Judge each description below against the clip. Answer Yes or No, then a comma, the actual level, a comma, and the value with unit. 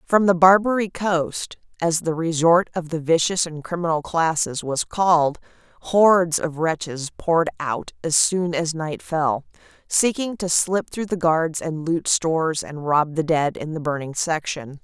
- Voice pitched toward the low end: No, medium, 165 Hz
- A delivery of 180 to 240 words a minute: No, average, 170 wpm